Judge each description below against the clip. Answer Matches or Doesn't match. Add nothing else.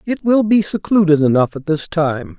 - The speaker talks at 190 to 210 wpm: Matches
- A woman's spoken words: Doesn't match